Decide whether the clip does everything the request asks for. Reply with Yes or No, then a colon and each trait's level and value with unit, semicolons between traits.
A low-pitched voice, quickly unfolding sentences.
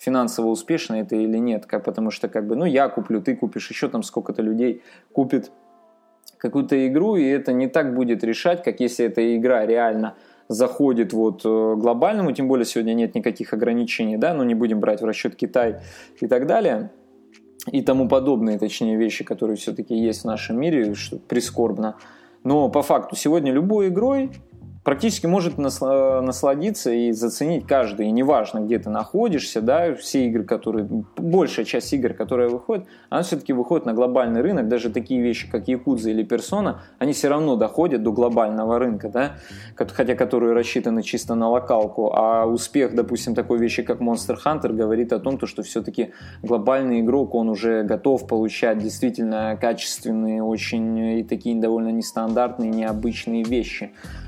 Yes: low, 115 Hz; fast, 165 wpm